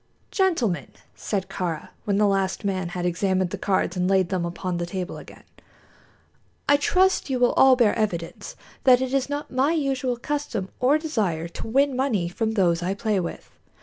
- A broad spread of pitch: Yes, wide, 6.3 semitones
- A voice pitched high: Yes, high, 205 Hz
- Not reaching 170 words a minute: No, average, 180 wpm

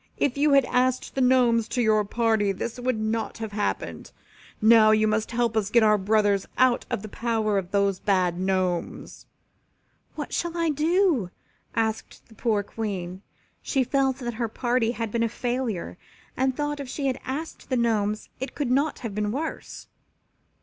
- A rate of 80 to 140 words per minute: No, average, 180 wpm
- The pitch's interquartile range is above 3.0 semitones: Yes, average, 3.4 semitones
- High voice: Yes, high, 230 Hz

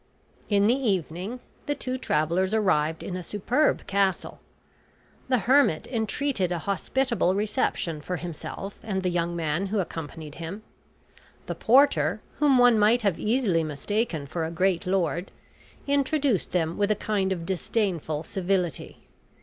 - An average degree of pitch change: Yes, average, 4.9 semitones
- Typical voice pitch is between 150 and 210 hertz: Yes, high, 190 Hz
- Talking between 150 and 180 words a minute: No, average, 140 wpm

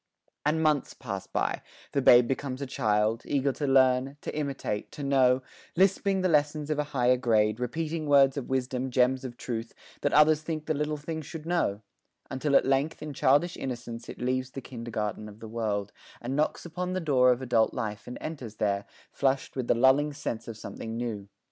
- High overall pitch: No, low, 130 Hz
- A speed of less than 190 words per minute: No, average, 195 wpm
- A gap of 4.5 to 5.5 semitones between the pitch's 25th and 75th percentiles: No, average, 4.1 semitones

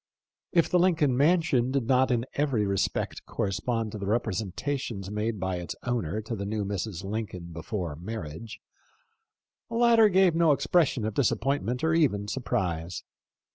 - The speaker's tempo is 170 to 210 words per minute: No, average, 150 wpm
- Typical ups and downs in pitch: No, wide, 6.2 semitones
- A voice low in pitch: Yes, low, 115 Hz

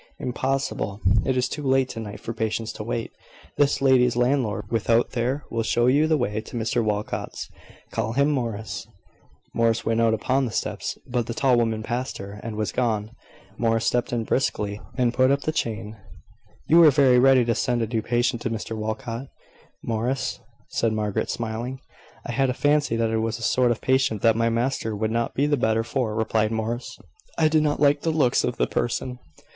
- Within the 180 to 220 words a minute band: Yes, average, 200 wpm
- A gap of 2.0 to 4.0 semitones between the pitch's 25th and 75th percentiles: Yes, average, 2.8 semitones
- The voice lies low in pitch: Yes, low, 120 Hz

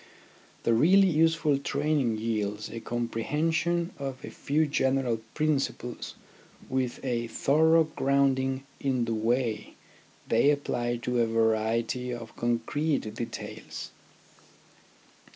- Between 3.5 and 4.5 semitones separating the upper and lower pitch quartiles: Yes, average, 4.2 semitones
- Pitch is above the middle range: No, low, 130 Hz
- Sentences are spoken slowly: Yes, slow, 105 wpm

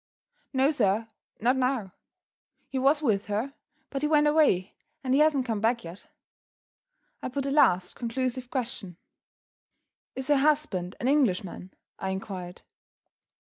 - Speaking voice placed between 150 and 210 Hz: No, very high, 250 Hz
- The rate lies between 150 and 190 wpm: No, average, 140 wpm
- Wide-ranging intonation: Yes, wide, 5.9 semitones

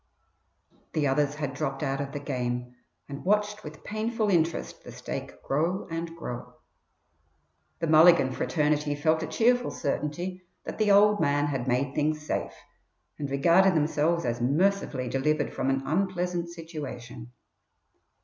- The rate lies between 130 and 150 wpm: Yes, average, 140 wpm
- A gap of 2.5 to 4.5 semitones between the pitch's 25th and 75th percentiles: Yes, average, 4.2 semitones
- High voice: No, medium, 155 Hz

